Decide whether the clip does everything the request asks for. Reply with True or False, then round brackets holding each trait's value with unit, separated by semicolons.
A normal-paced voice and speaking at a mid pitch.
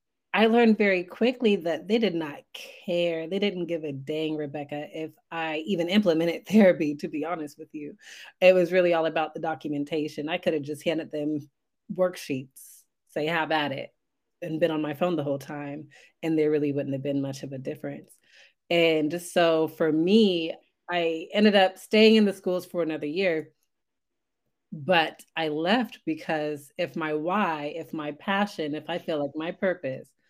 True (180 wpm; 165 Hz)